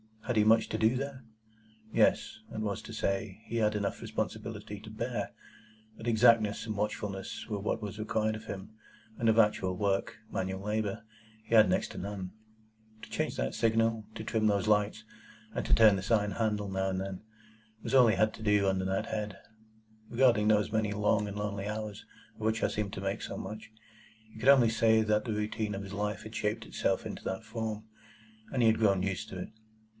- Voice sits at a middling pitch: No, low, 105 Hz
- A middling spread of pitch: No, narrow, 1.7 semitones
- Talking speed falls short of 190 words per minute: No, average, 200 wpm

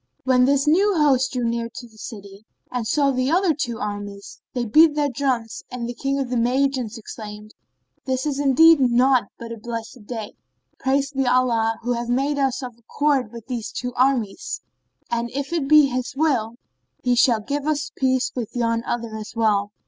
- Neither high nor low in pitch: No, very high, 250 Hz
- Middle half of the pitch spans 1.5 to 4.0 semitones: Yes, average, 3.1 semitones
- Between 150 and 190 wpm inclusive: Yes, average, 185 wpm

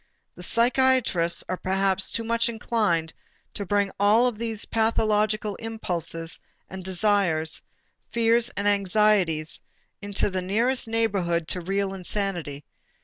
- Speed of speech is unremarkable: No, slow, 115 wpm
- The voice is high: Yes, high, 200 Hz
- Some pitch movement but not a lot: Yes, average, 3.8 semitones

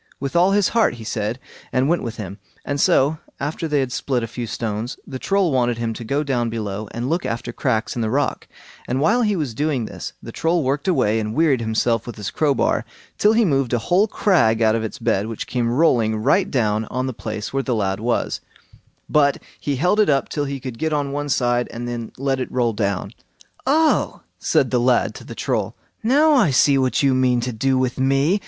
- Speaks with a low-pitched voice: Yes, low, 130 Hz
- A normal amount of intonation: Yes, average, 4.4 semitones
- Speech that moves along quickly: Yes, fast, 225 wpm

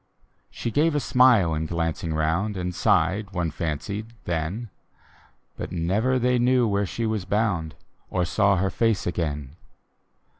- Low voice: Yes, very low, 95 Hz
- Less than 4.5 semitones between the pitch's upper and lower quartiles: No, average, 5.3 semitones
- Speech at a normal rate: Yes, average, 150 wpm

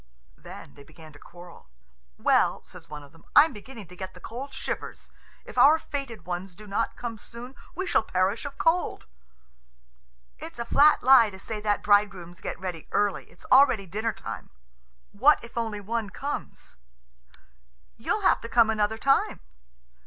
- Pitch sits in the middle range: No, high, 215 Hz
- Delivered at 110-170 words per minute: Yes, average, 165 wpm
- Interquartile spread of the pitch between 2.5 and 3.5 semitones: No, average, 4.8 semitones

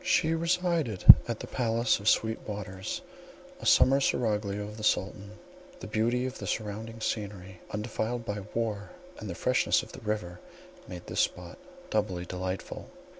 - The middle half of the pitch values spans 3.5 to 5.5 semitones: No, average, 2.7 semitones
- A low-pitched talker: Yes, low, 105 Hz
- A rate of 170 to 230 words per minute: No, average, 155 wpm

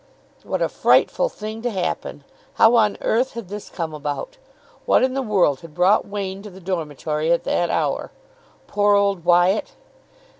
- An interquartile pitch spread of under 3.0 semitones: No, average, 4.0 semitones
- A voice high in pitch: Yes, high, 195 Hz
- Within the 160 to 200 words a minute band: Yes, average, 165 wpm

